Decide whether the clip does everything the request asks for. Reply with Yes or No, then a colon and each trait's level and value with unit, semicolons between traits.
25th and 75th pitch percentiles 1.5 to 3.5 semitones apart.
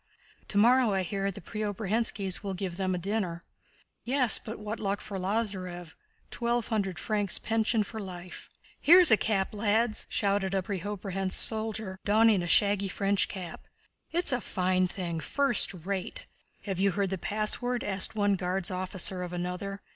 Yes: average, 2.7 semitones